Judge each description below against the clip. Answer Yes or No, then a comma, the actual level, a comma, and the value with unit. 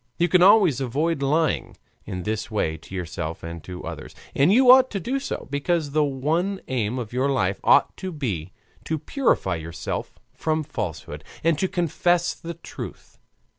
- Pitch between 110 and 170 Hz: Yes, medium, 140 Hz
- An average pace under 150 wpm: No, average, 170 wpm